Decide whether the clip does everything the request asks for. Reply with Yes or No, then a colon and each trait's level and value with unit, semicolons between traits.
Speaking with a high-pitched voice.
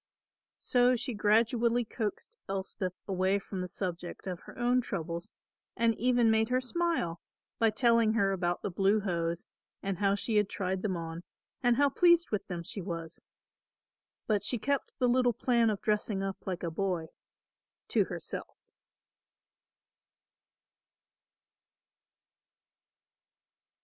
Yes: high, 205 Hz